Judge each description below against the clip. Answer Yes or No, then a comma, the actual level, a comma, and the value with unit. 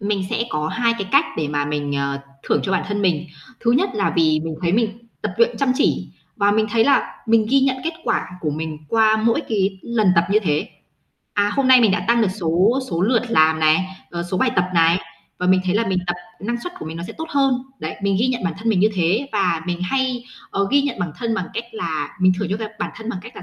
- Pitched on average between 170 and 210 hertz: Yes, high, 200 Hz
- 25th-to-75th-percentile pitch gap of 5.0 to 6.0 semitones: Yes, wide, 5.4 semitones